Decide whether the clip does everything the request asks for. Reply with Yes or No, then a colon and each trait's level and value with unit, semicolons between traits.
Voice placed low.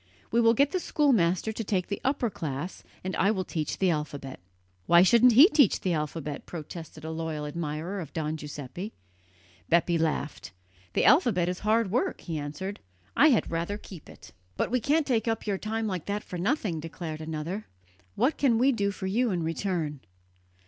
No: medium, 185 Hz